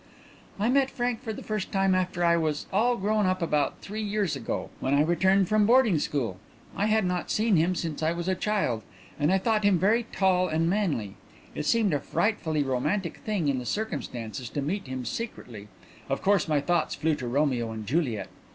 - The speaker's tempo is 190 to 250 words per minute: Yes, fast, 205 wpm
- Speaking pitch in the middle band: Yes, medium, 175 Hz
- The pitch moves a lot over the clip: Yes, wide, 6.2 semitones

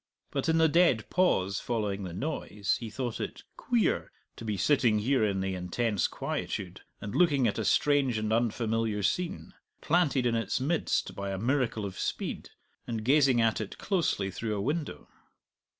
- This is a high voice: No, low, 115 Hz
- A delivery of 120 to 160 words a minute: No, average, 170 wpm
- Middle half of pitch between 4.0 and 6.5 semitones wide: Yes, wide, 5.6 semitones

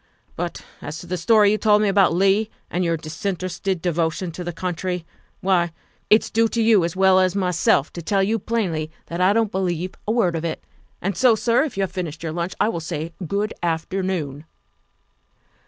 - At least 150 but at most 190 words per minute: No, average, 200 wpm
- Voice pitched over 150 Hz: Yes, medium, 185 Hz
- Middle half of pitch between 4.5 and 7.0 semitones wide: No, average, 3.2 semitones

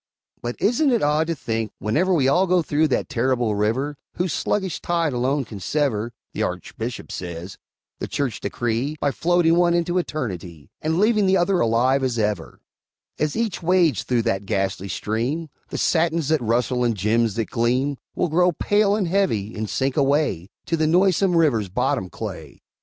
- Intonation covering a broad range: Yes, wide, 7.3 semitones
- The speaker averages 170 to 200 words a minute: Yes, average, 175 wpm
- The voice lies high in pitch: No, medium, 140 Hz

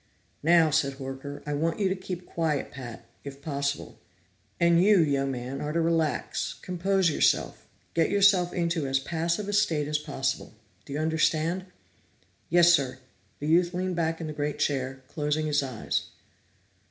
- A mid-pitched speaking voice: Yes, medium, 155 Hz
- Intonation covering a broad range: No, average, 3.6 semitones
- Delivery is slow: No, average, 165 wpm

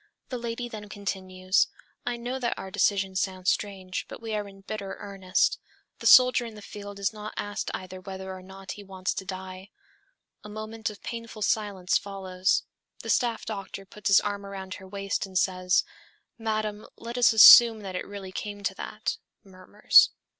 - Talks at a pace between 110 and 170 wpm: No, average, 180 wpm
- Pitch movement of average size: No, narrow, 2.2 semitones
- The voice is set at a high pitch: Yes, high, 200 Hz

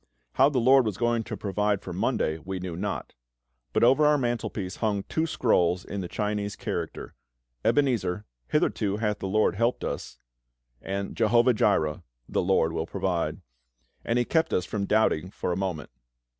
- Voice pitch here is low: Yes, low, 105 Hz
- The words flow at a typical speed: Yes, average, 170 wpm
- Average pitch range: Yes, average, 4.2 semitones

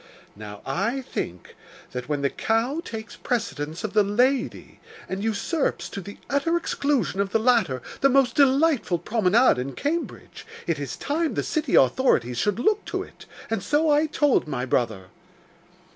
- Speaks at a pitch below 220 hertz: No, high, 225 Hz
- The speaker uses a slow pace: No, average, 160 wpm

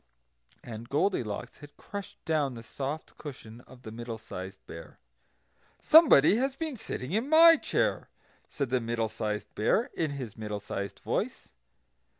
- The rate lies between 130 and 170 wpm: Yes, average, 150 wpm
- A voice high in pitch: No, low, 130 Hz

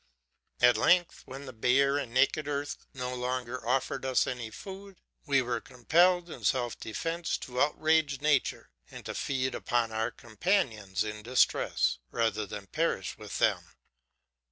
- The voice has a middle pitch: No, low, 130 Hz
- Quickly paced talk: No, average, 150 wpm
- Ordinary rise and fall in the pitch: Yes, average, 3.9 semitones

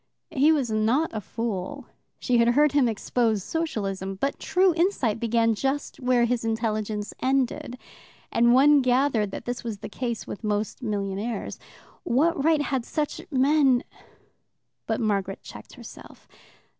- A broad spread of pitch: No, average, 4.3 semitones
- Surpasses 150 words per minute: No, average, 145 wpm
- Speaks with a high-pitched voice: Yes, high, 240 Hz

